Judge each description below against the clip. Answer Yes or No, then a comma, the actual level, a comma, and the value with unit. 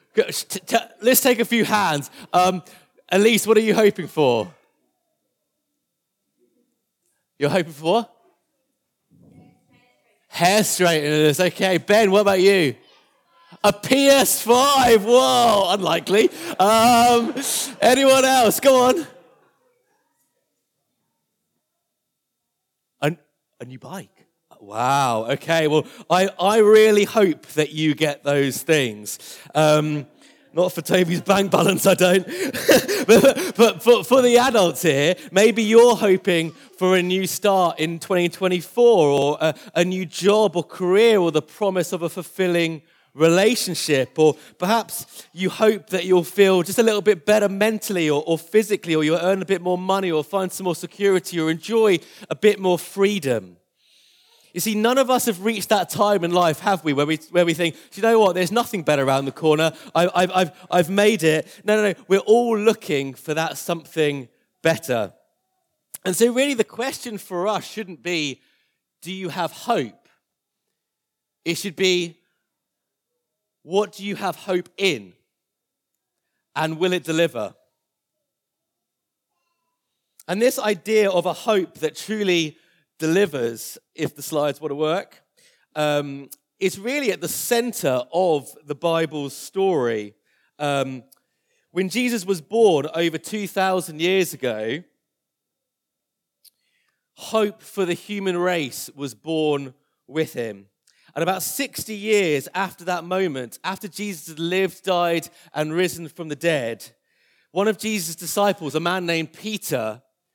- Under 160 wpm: Yes, average, 140 wpm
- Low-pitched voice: No, medium, 185 Hz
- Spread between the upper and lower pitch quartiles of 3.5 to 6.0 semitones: Yes, average, 5.0 semitones